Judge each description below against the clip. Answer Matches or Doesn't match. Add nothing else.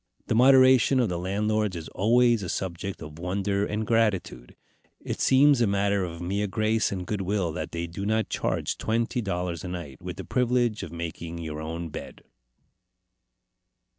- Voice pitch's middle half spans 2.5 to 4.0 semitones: Doesn't match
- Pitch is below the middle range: Matches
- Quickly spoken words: Doesn't match